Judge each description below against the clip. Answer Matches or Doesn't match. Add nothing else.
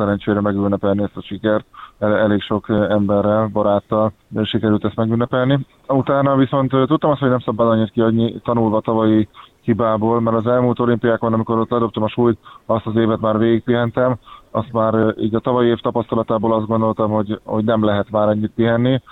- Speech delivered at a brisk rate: Matches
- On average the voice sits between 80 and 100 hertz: Doesn't match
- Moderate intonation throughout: Doesn't match